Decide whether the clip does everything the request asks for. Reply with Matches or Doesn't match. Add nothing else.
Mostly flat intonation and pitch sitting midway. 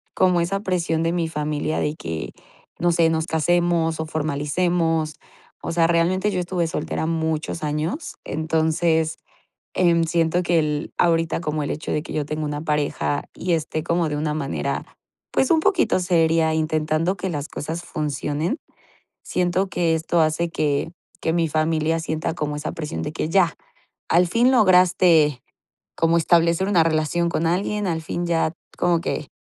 Matches